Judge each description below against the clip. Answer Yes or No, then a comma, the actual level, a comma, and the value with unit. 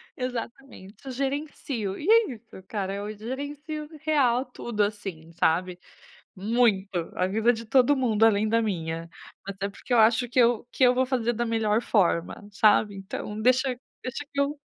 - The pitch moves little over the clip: No, average, 4.1 semitones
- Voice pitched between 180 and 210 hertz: No, high, 230 Hz